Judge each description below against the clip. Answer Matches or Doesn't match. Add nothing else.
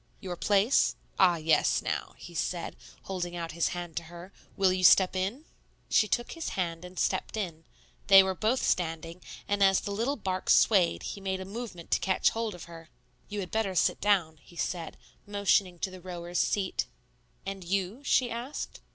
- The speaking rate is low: Doesn't match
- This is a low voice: Doesn't match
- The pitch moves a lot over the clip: Doesn't match